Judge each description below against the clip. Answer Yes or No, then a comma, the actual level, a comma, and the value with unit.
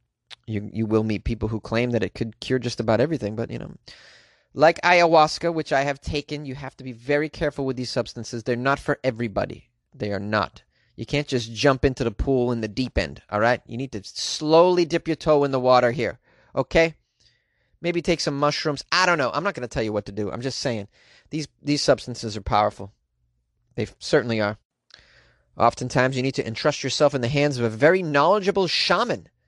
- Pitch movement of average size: Yes, average, 4.6 semitones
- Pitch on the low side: Yes, low, 125 Hz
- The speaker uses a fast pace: Yes, fast, 215 wpm